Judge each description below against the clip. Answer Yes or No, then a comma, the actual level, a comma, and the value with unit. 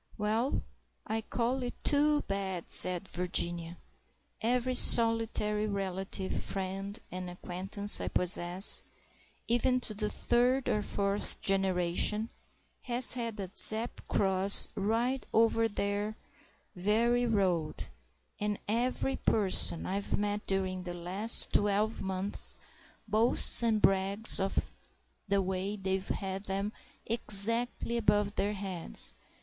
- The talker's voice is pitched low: No, high, 205 Hz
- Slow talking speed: Yes, slow, 115 wpm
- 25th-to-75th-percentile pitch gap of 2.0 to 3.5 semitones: Yes, average, 3.0 semitones